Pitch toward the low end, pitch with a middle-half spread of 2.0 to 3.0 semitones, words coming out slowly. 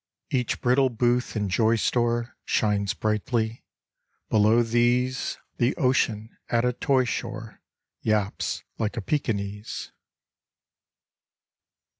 Yes: low, 115 Hz; narrow, 2.4 semitones; slow, 100 wpm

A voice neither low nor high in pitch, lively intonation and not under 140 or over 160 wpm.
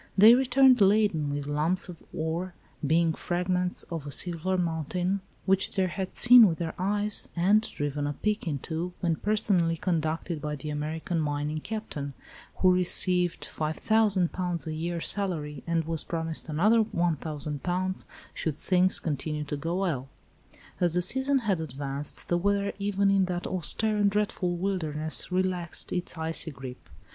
No: medium, 175 Hz; average, 3.6 semitones; average, 150 wpm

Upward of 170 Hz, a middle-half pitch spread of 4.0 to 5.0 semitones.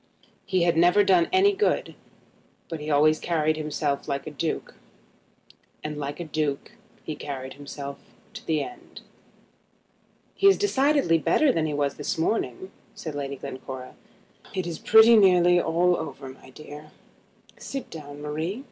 No: medium, 155 Hz; average, 4.3 semitones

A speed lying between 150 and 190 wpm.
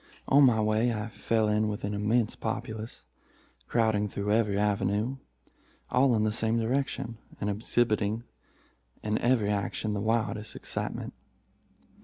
No: slow, 135 wpm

